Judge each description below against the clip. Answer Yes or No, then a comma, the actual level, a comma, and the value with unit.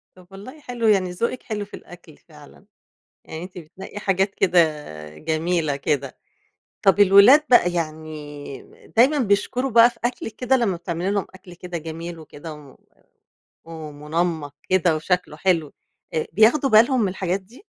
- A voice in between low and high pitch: Yes, medium, 180 Hz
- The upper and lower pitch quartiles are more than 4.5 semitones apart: Yes, average, 4.9 semitones